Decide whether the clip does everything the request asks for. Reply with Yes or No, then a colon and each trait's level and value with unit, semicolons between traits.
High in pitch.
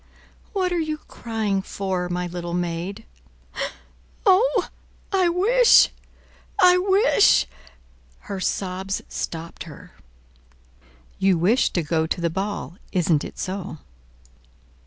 Yes: high, 195 Hz